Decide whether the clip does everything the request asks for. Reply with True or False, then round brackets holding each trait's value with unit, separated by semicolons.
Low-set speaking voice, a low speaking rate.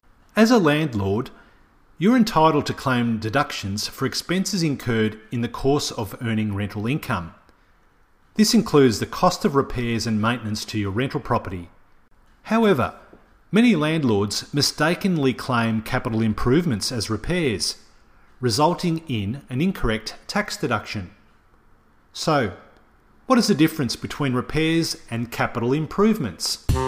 True (125 Hz; 125 wpm)